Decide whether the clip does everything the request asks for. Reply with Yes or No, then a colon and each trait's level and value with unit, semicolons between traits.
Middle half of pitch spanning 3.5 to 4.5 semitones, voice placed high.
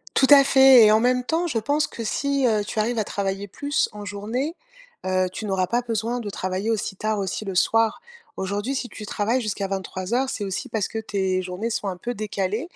Yes: average, 3.9 semitones; high, 215 Hz